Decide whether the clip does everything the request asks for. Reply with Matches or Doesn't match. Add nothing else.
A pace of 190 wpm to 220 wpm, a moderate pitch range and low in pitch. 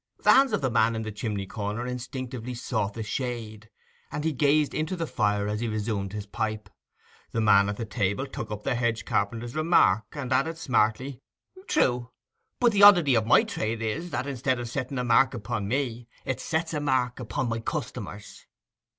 Matches